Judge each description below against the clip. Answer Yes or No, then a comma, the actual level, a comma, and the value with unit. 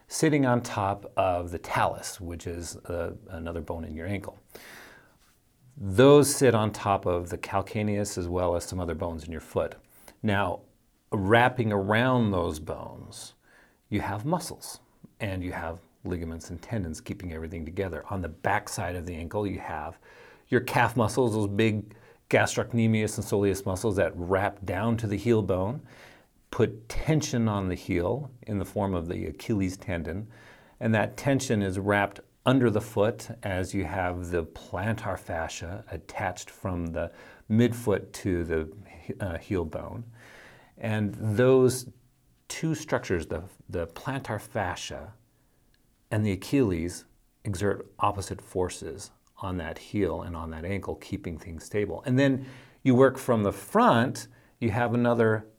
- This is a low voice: Yes, low, 100 Hz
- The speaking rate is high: No, average, 150 wpm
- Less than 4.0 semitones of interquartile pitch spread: No, average, 4.7 semitones